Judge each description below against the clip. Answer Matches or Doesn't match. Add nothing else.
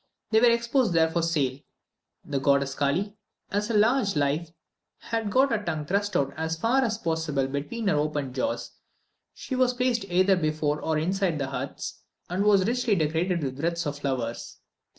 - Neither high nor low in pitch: Matches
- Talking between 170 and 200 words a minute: Matches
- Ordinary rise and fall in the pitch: Doesn't match